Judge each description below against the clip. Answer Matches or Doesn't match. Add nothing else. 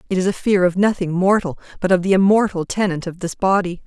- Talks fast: Matches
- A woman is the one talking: Matches